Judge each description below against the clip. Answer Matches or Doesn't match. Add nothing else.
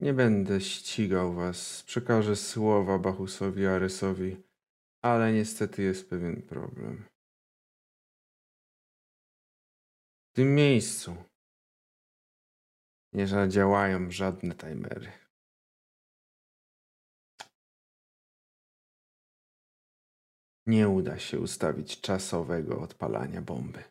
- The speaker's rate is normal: Doesn't match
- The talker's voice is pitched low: Matches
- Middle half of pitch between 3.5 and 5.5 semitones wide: Doesn't match